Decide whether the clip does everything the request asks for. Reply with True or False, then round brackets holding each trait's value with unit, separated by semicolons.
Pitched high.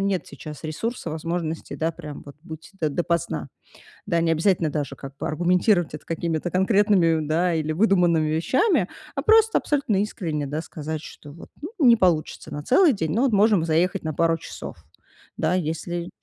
False (170 Hz)